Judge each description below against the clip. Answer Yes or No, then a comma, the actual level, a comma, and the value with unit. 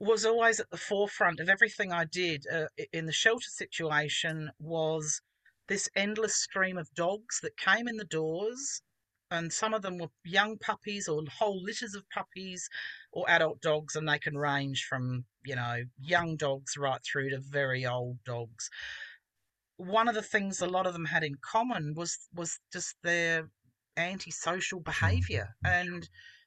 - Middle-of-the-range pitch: Yes, medium, 170 Hz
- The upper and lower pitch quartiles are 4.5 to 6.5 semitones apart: Yes, average, 5.0 semitones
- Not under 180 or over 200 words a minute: No, average, 170 wpm